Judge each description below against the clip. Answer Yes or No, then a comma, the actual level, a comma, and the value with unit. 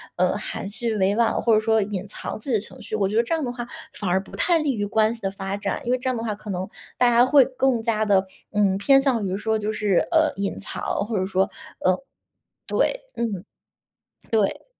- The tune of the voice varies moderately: Yes, average, 3.3 semitones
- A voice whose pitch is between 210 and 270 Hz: Yes, high, 215 Hz